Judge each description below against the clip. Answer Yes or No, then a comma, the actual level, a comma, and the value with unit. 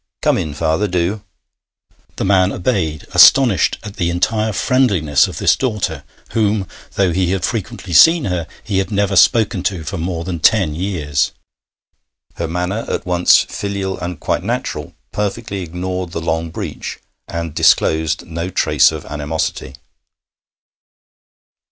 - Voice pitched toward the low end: Yes, very low, 90 Hz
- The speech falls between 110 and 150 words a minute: Yes, average, 140 wpm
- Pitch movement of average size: Yes, average, 3.5 semitones